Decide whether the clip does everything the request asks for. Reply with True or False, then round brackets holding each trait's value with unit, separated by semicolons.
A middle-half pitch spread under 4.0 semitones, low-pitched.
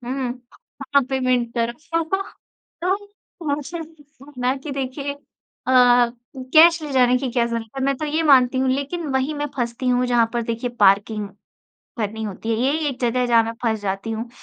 False (3.4 semitones; 255 Hz)